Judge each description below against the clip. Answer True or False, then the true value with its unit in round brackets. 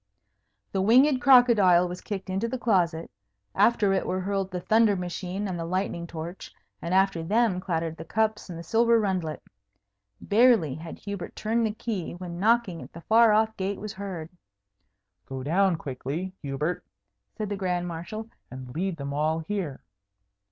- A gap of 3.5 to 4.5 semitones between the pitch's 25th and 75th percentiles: True (4.2 semitones)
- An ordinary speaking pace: True (165 wpm)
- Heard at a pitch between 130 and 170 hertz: False (190 Hz)